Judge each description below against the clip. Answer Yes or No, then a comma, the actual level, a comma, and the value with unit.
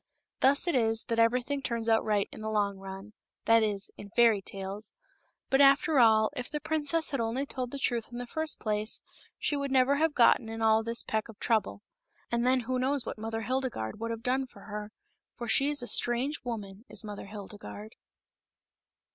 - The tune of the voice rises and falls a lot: No, average, 3.4 semitones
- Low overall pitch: No, high, 230 Hz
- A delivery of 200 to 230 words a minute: Yes, fast, 205 wpm